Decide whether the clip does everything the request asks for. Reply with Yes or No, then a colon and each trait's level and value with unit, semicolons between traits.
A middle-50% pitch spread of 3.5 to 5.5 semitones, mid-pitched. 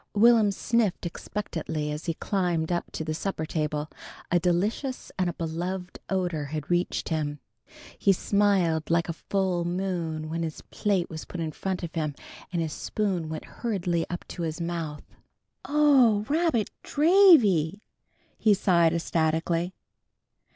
Yes: average, 3.8 semitones; medium, 175 Hz